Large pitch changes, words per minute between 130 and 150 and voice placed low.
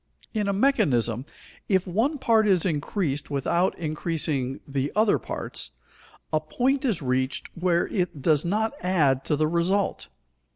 No: wide, 5.9 semitones; average, 140 wpm; medium, 170 Hz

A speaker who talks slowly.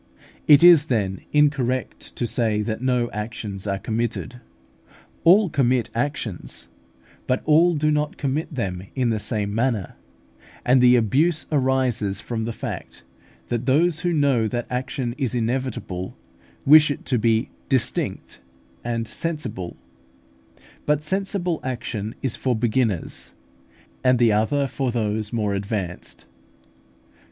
Yes: slow, 130 wpm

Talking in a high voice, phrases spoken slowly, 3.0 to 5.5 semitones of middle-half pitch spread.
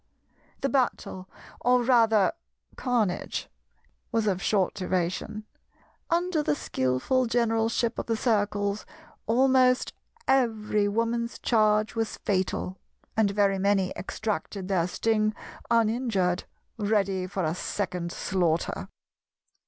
Yes: high, 215 Hz; slow, 105 wpm; average, 3.6 semitones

